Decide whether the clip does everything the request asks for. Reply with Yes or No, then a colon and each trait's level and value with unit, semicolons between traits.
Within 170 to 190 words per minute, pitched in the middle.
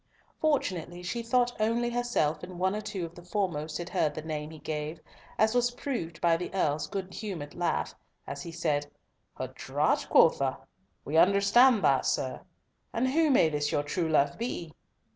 Yes: average, 180 wpm; medium, 175 Hz